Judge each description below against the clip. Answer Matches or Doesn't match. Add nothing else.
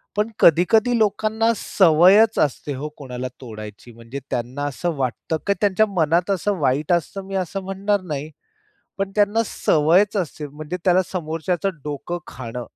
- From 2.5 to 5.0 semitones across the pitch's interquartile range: Doesn't match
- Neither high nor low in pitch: Matches